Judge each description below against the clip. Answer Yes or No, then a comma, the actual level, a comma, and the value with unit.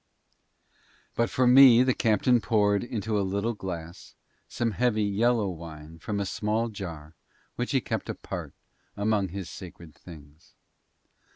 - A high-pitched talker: No, low, 100 Hz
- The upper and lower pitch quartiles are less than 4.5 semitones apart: No, average, 4.9 semitones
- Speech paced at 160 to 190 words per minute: No, slow, 135 wpm